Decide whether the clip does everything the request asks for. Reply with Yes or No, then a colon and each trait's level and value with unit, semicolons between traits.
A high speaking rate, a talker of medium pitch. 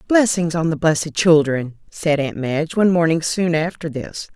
No: average, 180 wpm; medium, 160 Hz